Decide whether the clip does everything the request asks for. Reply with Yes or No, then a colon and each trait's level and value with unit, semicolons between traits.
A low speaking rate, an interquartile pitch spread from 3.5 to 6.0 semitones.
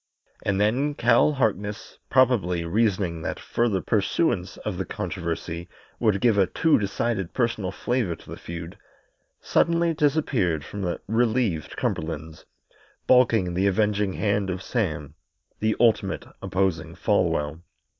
Yes: slow, 125 wpm; average, 5.2 semitones